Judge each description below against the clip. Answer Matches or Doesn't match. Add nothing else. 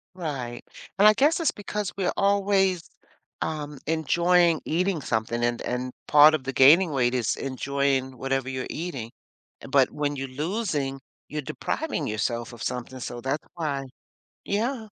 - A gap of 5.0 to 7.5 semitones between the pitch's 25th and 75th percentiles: Matches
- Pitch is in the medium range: Matches